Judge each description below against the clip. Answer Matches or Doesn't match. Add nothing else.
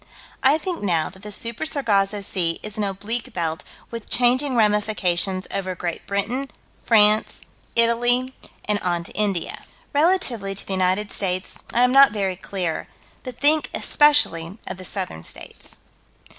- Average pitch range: Matches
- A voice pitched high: Matches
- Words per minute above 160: Doesn't match